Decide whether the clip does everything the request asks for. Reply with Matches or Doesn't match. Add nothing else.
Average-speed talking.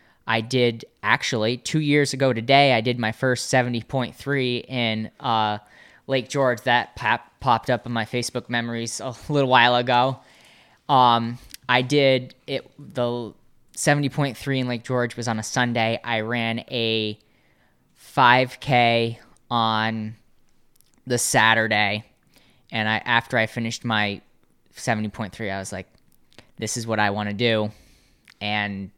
Matches